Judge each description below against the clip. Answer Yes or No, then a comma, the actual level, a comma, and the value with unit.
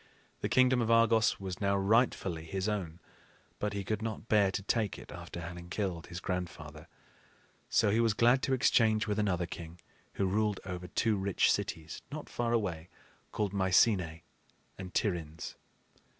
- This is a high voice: No, low, 100 Hz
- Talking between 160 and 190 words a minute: Yes, average, 165 wpm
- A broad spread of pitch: No, average, 3.8 semitones